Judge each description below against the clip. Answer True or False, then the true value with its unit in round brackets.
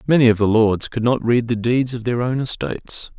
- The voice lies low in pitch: True (120 Hz)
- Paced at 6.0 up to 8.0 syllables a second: False (5.4 syllables/s)